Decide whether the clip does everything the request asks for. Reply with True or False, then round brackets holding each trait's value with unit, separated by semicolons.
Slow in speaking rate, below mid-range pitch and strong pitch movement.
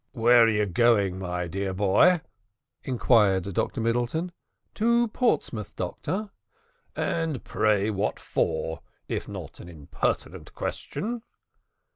True (110 wpm; 110 Hz; 7.7 semitones)